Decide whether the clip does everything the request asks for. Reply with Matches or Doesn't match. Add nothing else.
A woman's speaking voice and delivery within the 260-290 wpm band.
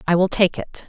Matches